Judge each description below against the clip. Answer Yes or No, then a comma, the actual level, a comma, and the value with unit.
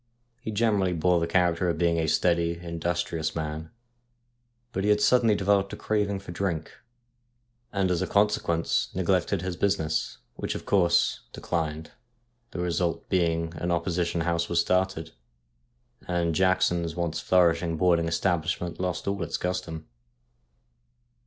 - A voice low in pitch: Yes, very low, 85 Hz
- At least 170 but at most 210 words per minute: No, slow, 135 wpm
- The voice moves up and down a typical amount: No, narrow, 2.1 semitones